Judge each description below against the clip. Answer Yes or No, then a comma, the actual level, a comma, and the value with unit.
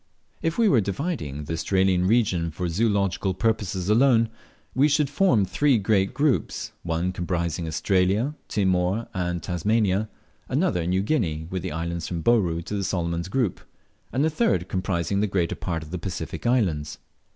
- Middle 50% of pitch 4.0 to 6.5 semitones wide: Yes, average, 4.7 semitones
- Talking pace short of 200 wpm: Yes, average, 160 wpm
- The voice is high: No, very low, 95 Hz